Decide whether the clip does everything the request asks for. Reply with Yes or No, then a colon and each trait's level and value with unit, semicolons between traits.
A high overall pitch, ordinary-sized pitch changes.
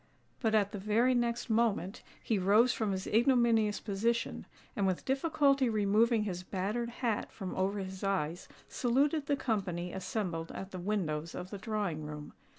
Yes: high, 210 Hz; average, 3.8 semitones